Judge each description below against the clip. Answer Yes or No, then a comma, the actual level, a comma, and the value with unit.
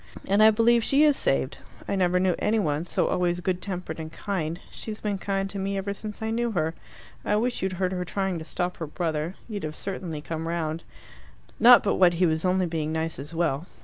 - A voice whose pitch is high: No, medium, 180 Hz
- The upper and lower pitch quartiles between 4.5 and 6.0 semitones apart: No, average, 3.7 semitones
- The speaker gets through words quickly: Yes, fast, 225 wpm